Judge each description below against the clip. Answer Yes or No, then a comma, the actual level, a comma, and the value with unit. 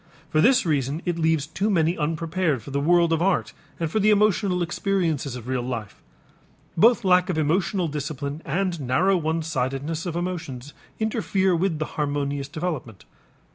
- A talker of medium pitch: Yes, medium, 165 Hz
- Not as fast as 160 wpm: No, average, 165 wpm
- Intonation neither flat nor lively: Yes, average, 4.2 semitones